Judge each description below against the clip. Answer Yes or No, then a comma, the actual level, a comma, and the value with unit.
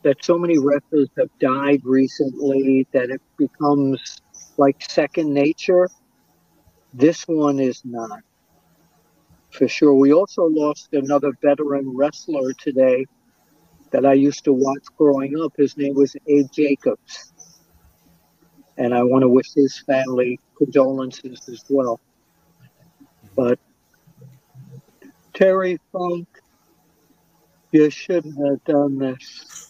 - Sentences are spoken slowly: Yes, slow, 115 wpm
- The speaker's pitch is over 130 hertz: Yes, medium, 140 Hz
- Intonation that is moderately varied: No, narrow, 2.1 semitones